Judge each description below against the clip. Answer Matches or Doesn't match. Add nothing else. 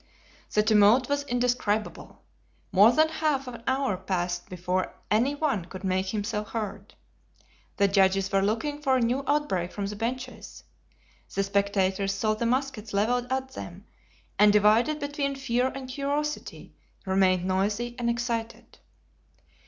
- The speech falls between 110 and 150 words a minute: Matches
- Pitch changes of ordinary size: Matches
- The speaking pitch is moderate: Doesn't match